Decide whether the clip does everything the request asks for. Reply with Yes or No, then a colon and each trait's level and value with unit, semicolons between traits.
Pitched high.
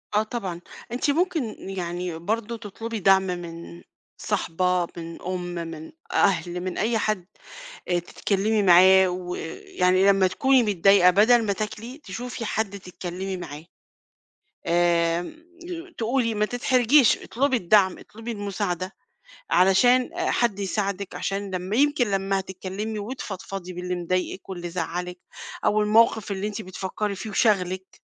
Yes: high, 195 Hz